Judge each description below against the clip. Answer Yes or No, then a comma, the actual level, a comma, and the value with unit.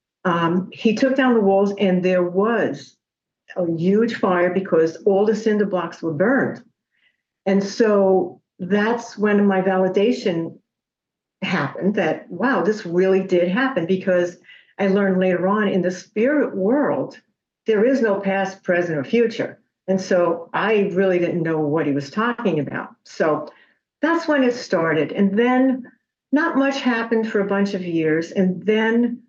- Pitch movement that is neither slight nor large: Yes, average, 4.0 semitones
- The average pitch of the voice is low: No, high, 195 Hz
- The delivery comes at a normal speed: Yes, average, 155 wpm